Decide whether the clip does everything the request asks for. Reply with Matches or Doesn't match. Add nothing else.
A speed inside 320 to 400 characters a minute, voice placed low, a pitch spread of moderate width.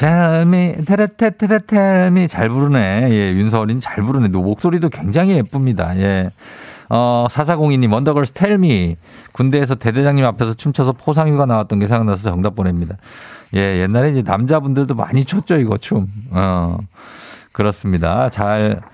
Doesn't match